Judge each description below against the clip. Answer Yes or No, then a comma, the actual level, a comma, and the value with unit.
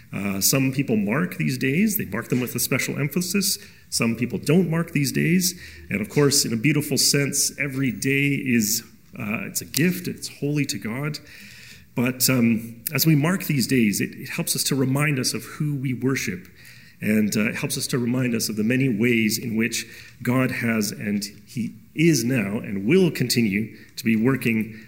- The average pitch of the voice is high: No, low, 130 Hz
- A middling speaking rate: Yes, average, 195 wpm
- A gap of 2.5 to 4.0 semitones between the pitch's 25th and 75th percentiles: No, average, 4.7 semitones